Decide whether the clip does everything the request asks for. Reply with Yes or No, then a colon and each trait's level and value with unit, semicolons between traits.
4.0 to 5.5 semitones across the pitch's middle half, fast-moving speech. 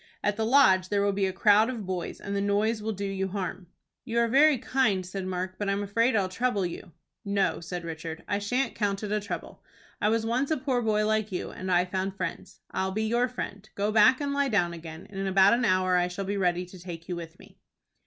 No: average, 3.0 semitones; fast, 245 wpm